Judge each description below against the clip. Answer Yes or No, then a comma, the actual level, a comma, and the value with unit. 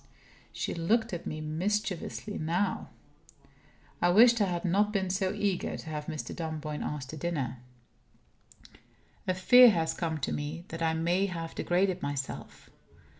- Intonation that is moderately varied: Yes, average, 3.7 semitones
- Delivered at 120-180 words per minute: Yes, average, 150 wpm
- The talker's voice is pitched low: No, medium, 175 Hz